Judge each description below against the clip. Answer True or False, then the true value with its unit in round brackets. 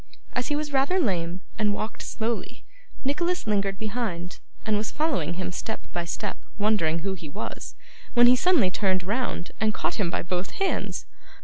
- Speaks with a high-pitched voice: True (210 Hz)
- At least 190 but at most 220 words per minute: False (175 wpm)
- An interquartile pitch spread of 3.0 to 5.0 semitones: False (5.6 semitones)